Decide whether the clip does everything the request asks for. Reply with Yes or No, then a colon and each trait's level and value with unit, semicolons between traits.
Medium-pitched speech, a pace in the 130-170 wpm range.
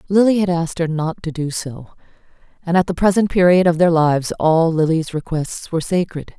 No: medium, 170 Hz; average, 195 wpm